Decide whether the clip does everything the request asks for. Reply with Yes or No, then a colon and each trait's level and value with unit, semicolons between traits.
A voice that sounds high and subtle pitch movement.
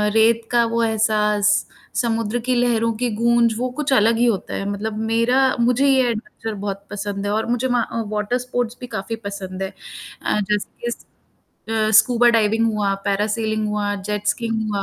Yes: high, 225 Hz; narrow, 2.3 semitones